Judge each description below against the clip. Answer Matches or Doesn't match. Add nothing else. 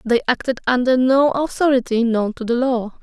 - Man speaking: Doesn't match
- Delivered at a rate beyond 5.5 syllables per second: Doesn't match